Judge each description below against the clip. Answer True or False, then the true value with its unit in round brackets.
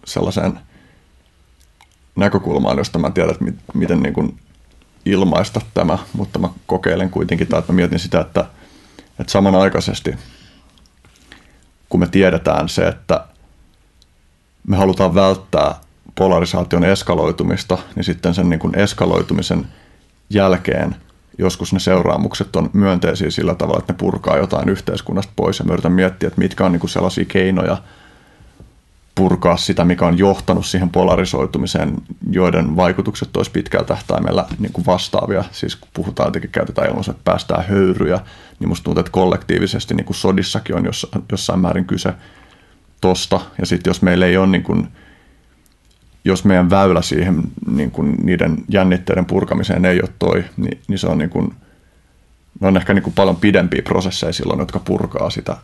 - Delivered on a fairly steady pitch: True (1.8 semitones)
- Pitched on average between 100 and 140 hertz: False (90 Hz)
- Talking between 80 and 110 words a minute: False (145 wpm)